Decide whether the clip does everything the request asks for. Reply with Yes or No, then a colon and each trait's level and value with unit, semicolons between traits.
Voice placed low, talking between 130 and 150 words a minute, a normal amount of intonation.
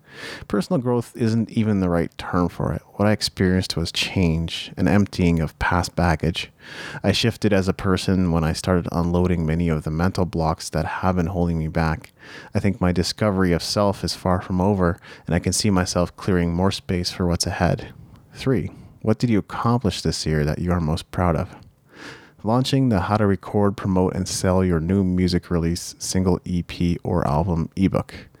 No: very low, 90 Hz; average, 190 wpm; average, 3.2 semitones